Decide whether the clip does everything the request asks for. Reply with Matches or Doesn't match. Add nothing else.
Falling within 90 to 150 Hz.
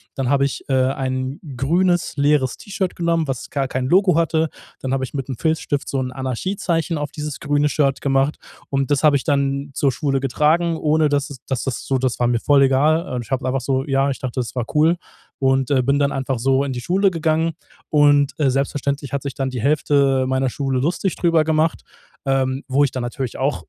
Matches